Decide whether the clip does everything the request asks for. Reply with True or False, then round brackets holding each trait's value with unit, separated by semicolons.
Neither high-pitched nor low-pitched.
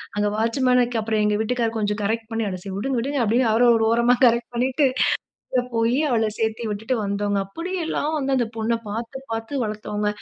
False (230 Hz)